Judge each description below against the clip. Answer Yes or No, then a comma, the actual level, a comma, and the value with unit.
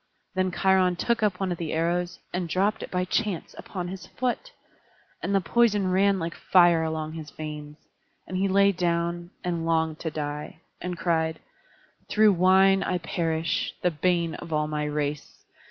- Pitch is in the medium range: Yes, medium, 175 Hz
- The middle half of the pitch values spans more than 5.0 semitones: No, average, 2.8 semitones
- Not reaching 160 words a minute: No, average, 170 wpm